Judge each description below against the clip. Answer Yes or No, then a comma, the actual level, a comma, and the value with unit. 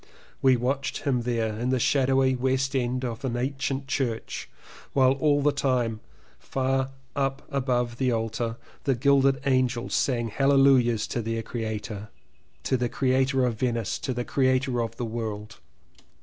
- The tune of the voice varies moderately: No, narrow, 2.3 semitones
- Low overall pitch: Yes, low, 130 Hz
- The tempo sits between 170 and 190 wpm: No, average, 150 wpm